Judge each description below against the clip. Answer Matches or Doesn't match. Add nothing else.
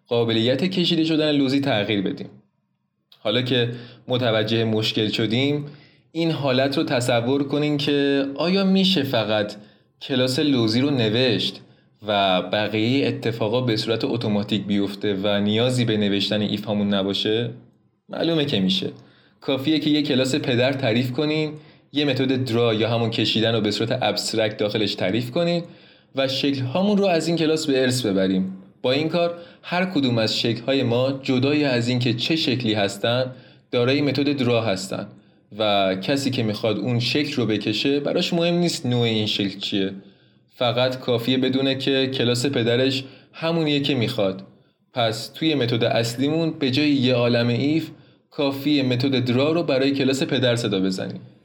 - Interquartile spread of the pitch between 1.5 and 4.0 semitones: Doesn't match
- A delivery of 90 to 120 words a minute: Doesn't match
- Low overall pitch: Matches